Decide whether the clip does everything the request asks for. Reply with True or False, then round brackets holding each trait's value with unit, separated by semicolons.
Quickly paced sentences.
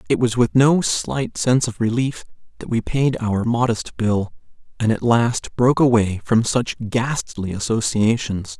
False (160 wpm)